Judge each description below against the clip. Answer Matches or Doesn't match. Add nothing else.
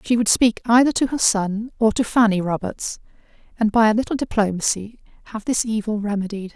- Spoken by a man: Doesn't match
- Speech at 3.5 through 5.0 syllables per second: Doesn't match